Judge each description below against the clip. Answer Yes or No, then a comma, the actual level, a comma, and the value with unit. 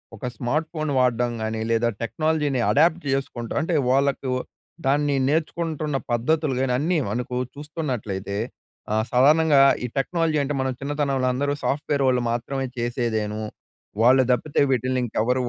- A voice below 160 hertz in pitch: Yes, low, 135 Hz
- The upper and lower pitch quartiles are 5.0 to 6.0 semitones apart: No, average, 3.8 semitones